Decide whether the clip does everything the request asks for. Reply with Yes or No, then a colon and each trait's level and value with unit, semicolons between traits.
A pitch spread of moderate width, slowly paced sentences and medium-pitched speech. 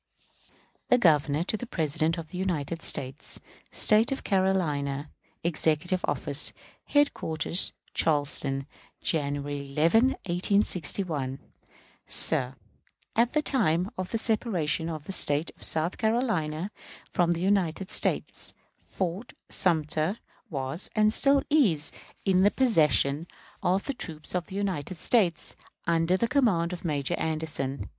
Yes: average, 4.6 semitones; slow, 125 wpm; medium, 170 Hz